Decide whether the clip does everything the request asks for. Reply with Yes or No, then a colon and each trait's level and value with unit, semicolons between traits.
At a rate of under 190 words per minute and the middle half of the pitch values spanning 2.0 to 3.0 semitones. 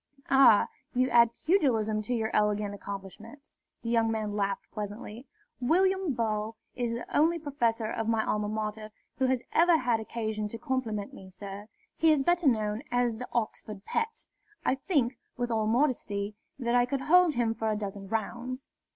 No: average, 170 wpm; average, 3.6 semitones